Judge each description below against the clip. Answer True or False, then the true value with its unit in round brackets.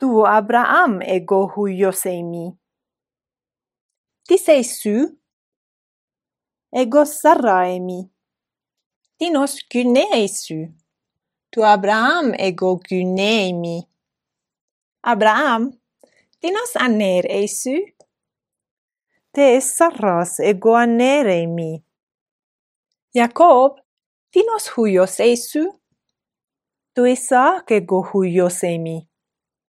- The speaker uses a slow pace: True (80 wpm)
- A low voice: False (225 Hz)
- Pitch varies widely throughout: True (6.9 semitones)